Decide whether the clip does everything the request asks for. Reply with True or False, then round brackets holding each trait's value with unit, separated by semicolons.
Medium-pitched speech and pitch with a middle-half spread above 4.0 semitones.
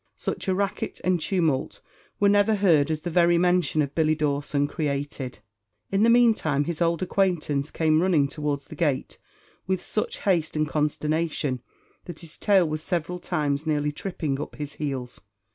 False (155 Hz; 3.5 semitones)